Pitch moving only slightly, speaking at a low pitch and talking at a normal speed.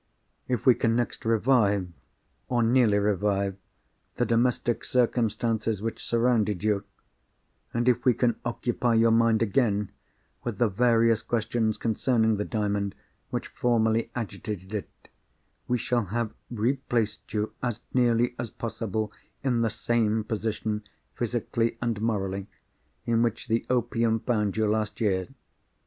No: narrow, 2.1 semitones; low, 115 Hz; slow, 130 wpm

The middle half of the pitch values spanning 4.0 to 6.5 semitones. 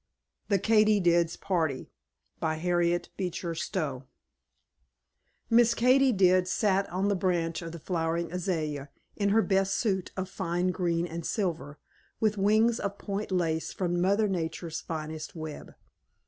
No: average, 3.3 semitones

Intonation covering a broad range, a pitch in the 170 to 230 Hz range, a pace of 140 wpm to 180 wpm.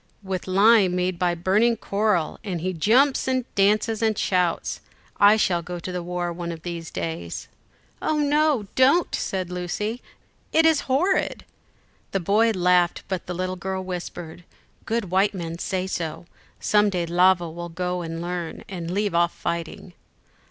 No: average, 3.4 semitones; medium, 185 Hz; average, 160 wpm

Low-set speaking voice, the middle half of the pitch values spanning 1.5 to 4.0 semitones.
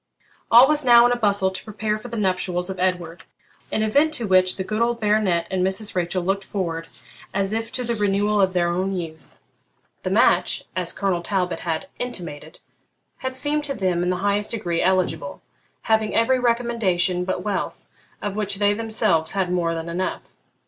No: high, 195 Hz; average, 3.5 semitones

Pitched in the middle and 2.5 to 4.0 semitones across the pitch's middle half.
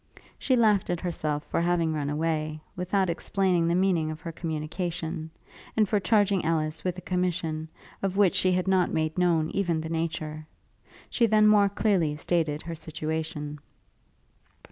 Yes: medium, 170 Hz; average, 3.0 semitones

